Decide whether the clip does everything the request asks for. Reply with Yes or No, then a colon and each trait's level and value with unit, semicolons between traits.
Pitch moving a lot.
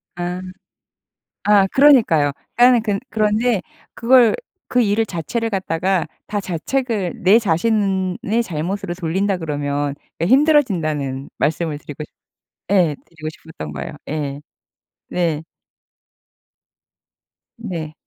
Yes: wide, 5.7 semitones